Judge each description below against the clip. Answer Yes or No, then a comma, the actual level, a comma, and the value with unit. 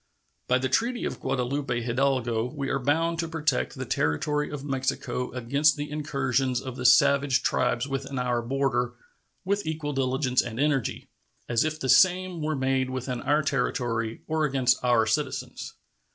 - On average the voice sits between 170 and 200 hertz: No, low, 135 Hz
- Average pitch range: Yes, average, 3.0 semitones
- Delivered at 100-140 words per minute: No, average, 160 wpm